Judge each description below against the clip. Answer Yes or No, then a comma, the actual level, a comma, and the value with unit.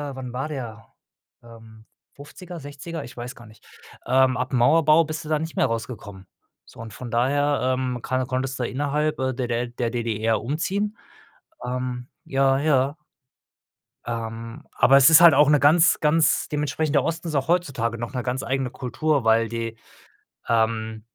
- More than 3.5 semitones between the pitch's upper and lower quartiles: Yes, average, 4.1 semitones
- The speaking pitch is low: Yes, low, 130 Hz